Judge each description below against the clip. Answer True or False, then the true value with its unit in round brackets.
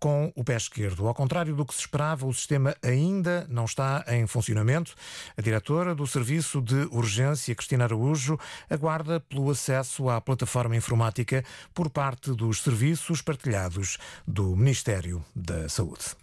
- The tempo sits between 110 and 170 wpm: True (150 wpm)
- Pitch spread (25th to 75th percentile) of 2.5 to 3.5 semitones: False (4.3 semitones)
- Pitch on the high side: False (130 Hz)